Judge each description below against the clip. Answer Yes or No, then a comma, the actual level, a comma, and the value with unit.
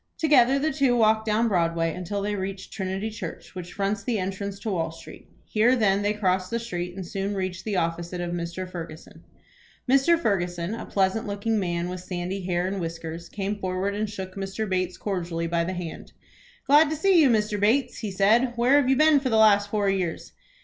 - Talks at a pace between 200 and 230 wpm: Yes, fast, 205 wpm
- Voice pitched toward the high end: Yes, high, 195 Hz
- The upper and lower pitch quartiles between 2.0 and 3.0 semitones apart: No, average, 3.6 semitones